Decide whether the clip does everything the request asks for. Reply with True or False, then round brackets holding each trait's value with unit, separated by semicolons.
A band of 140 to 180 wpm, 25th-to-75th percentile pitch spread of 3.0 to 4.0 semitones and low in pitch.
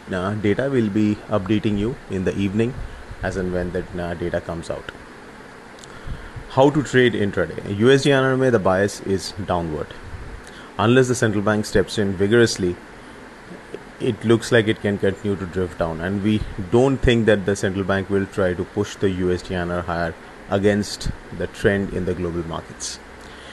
True (165 wpm; 3.3 semitones; 100 Hz)